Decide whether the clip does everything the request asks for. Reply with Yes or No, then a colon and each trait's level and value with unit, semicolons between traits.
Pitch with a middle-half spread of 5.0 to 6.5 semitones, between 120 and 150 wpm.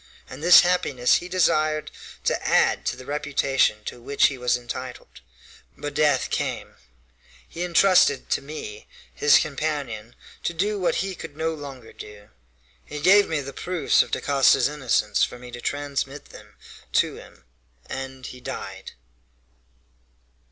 No: average, 3.9 semitones; average, 145 wpm